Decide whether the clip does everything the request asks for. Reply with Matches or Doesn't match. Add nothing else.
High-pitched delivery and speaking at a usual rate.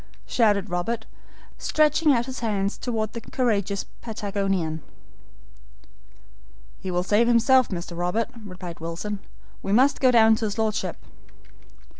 Doesn't match